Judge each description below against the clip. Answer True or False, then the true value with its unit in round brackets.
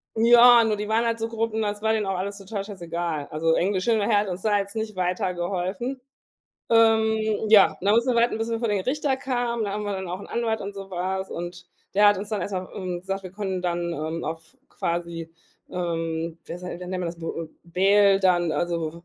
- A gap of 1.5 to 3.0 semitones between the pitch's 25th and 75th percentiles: False (4.0 semitones)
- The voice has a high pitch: True (195 Hz)